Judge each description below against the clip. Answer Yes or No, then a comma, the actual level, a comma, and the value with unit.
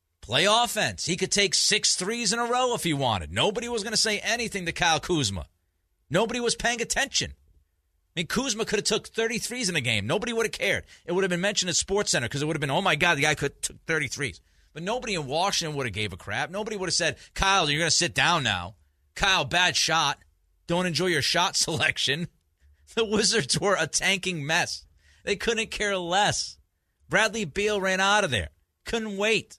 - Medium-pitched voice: Yes, medium, 175 Hz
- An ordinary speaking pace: No, fast, 215 wpm